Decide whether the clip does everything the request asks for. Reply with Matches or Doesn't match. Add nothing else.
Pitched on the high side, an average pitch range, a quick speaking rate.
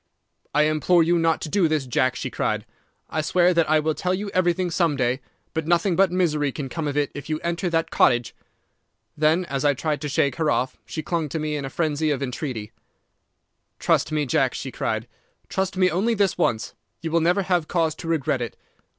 Doesn't match